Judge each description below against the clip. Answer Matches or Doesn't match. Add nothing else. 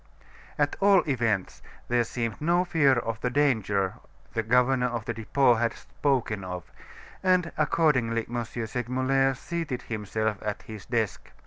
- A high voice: Doesn't match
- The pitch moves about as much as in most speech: Matches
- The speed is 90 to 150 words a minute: Matches